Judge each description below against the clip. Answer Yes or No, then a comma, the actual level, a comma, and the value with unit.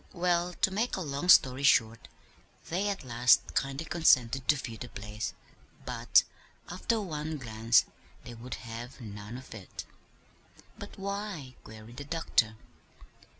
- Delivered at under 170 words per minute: Yes, average, 140 wpm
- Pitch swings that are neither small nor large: No, wide, 6.8 semitones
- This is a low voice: Yes, low, 130 Hz